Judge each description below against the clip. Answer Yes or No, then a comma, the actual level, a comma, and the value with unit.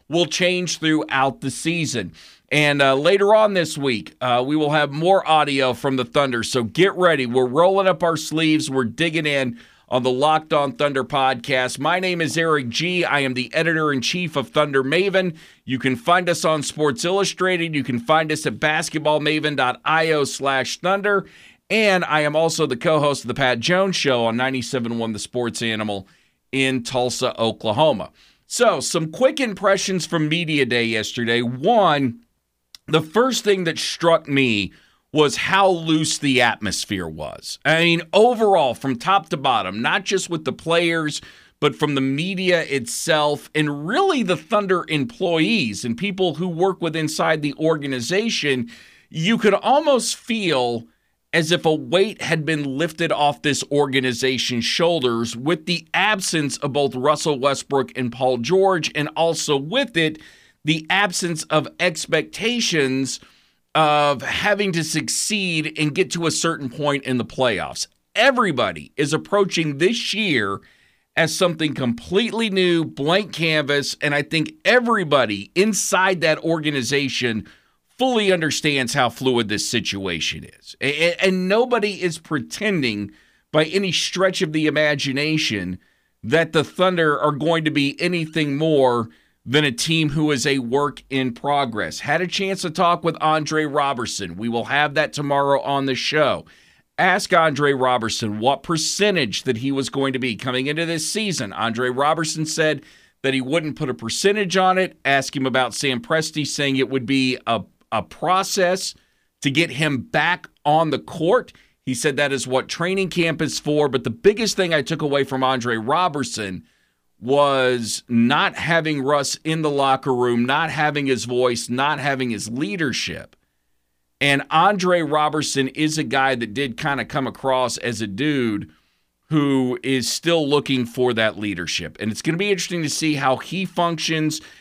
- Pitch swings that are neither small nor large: Yes, average, 4.6 semitones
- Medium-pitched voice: Yes, medium, 150 Hz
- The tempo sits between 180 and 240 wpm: No, average, 160 wpm